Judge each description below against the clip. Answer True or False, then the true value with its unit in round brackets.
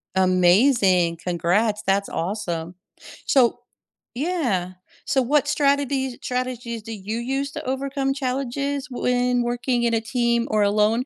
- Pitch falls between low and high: False (240 Hz)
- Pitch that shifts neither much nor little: True (4.6 semitones)